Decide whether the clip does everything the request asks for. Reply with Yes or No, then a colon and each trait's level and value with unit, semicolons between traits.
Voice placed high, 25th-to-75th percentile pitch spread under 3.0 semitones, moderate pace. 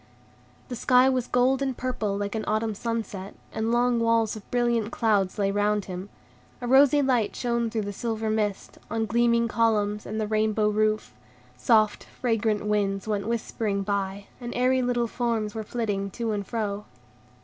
Yes: high, 220 Hz; narrow, 2.4 semitones; average, 170 wpm